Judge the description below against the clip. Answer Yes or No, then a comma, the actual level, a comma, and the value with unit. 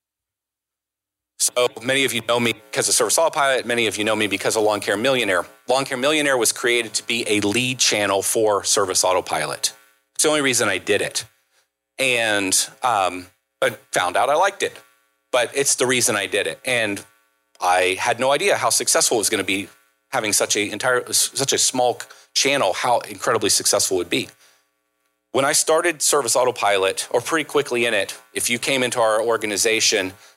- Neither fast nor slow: Yes, average, 190 wpm